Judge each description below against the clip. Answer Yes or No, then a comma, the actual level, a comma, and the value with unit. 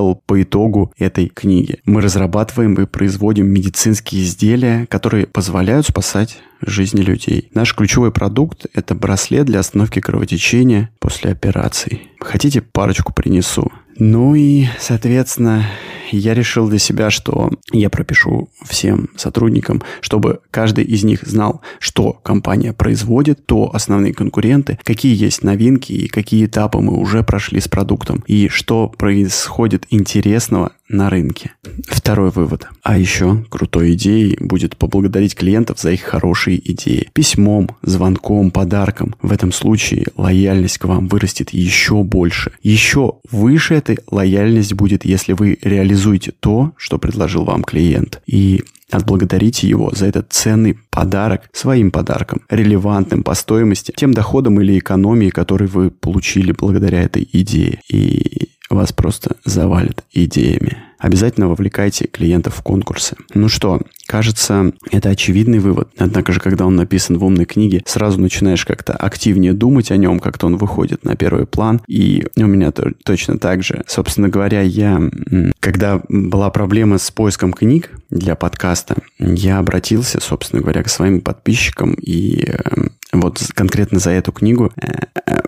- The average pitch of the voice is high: No, low, 100 Hz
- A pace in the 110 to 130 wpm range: No, average, 140 wpm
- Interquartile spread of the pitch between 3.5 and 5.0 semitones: No, average, 2.8 semitones